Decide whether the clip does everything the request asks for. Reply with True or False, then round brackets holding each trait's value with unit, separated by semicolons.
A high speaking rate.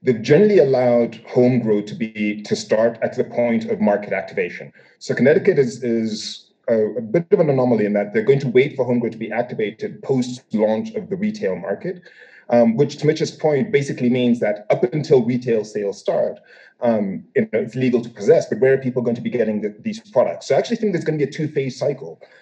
True (230 wpm)